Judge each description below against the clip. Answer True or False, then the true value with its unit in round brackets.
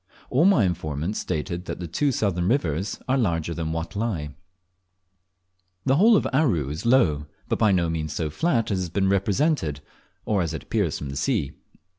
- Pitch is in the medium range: False (90 Hz)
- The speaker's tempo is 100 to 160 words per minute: False (185 wpm)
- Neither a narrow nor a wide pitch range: False (6.7 semitones)